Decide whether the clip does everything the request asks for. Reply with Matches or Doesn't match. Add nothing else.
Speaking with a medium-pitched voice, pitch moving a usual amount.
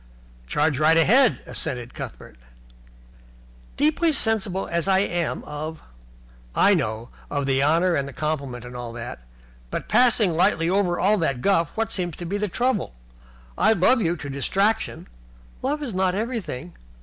Doesn't match